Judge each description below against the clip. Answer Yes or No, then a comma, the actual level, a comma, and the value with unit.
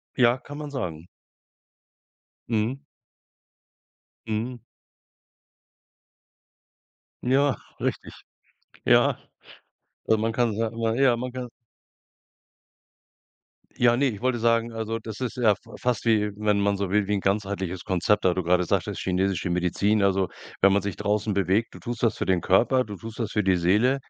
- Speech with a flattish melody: No, average, 3.5 semitones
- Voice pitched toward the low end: Yes, low, 105 Hz